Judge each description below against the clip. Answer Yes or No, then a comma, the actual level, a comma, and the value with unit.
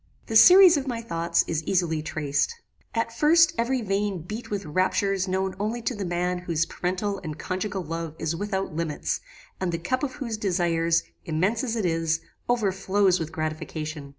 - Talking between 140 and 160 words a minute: No, average, 175 wpm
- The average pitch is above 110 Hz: Yes, medium, 185 Hz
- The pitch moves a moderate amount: Yes, average, 4.7 semitones